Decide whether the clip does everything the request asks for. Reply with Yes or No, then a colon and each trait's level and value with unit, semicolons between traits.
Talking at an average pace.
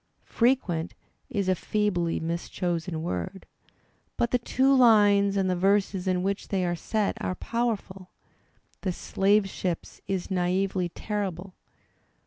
No: slow, 125 wpm